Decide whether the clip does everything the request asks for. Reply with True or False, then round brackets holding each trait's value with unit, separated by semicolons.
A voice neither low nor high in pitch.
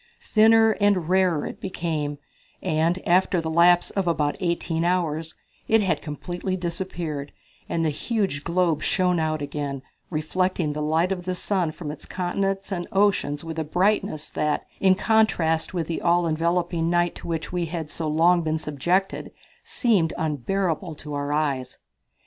True (170 Hz)